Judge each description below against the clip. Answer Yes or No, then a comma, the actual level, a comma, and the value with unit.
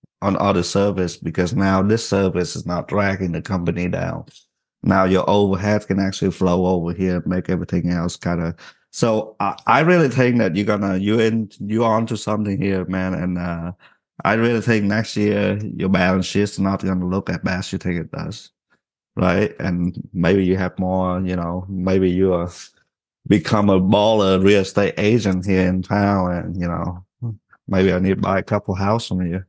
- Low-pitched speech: Yes, very low, 95 Hz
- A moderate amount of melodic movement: No, narrow, 2.2 semitones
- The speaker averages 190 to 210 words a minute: Yes, average, 200 wpm